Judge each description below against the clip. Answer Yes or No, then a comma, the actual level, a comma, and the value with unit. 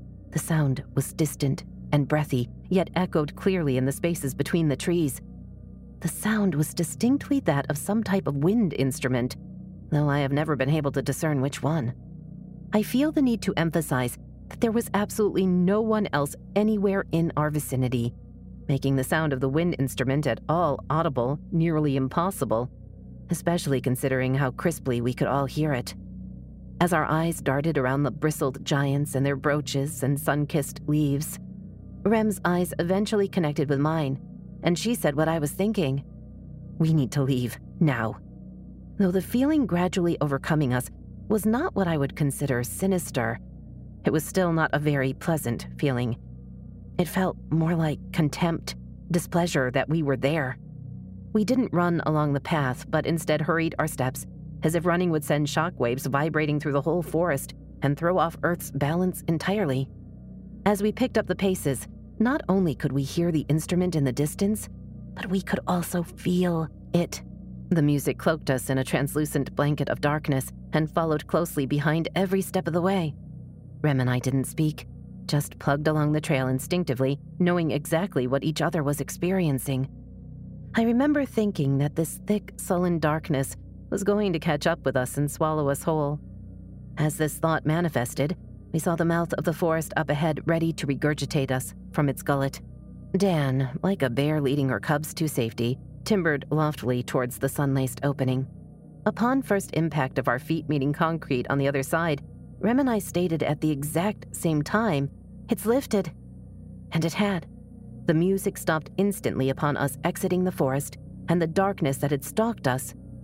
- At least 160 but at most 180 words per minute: Yes, average, 170 wpm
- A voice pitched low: No, medium, 155 Hz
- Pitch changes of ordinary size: Yes, average, 4.2 semitones